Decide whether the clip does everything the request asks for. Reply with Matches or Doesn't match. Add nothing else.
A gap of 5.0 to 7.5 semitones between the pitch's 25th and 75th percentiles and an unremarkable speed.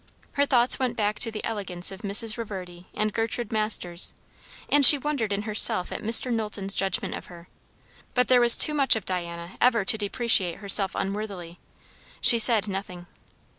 Doesn't match